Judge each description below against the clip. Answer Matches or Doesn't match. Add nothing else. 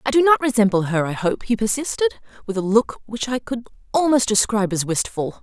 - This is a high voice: Matches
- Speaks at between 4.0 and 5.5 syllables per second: Doesn't match